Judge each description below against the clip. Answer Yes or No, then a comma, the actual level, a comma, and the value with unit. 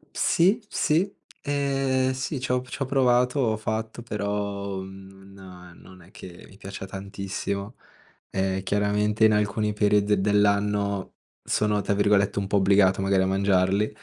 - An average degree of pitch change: No, narrow, 2.3 semitones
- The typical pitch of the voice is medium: No, low, 100 Hz